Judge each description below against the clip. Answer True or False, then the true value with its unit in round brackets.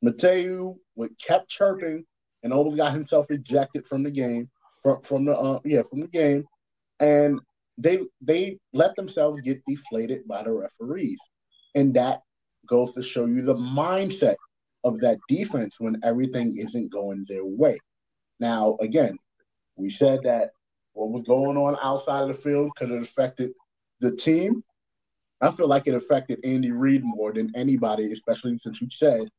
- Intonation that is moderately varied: True (3.7 semitones)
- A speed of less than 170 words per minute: True (160 wpm)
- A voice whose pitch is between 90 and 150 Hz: True (135 Hz)